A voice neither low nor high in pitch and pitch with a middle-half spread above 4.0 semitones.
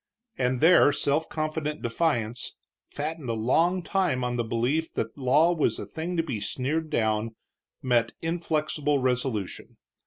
Yes: medium, 145 Hz; average, 5.0 semitones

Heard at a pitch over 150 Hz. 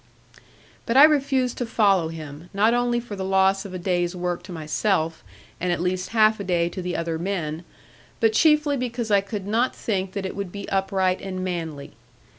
Yes: high, 190 Hz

